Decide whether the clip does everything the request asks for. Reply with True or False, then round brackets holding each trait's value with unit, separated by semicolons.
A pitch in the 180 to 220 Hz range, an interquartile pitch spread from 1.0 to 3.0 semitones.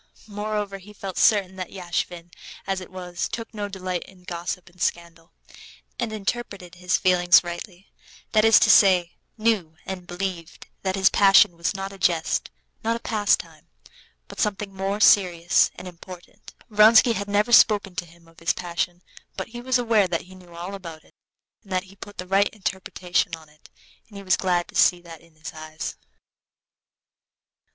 True (185 Hz; 2.7 semitones)